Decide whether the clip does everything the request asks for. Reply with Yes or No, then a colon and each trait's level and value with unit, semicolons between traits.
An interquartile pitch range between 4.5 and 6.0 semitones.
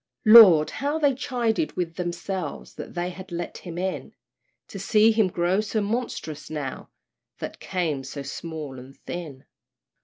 Yes: wide, 5.5 semitones